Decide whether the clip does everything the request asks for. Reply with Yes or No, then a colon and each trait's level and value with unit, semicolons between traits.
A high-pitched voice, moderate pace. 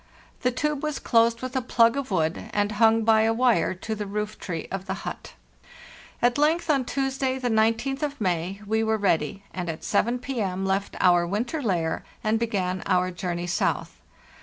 Yes: high, 220 Hz; average, 185 wpm